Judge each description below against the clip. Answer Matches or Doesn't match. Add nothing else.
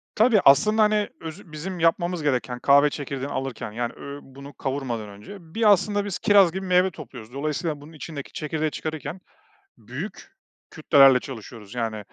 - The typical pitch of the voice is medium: Matches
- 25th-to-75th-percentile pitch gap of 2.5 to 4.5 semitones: Doesn't match